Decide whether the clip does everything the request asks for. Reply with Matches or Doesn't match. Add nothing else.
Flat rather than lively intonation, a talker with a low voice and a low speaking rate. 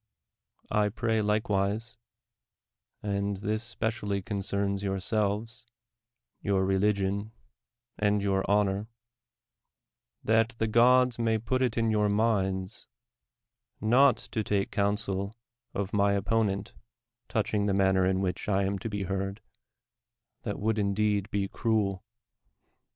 Matches